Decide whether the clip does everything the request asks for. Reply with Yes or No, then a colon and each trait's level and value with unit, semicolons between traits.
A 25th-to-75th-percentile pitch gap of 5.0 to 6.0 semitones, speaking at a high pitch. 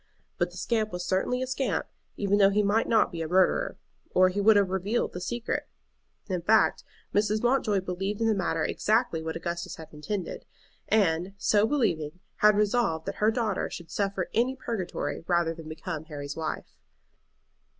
No: average, 4.2 semitones; high, 195 Hz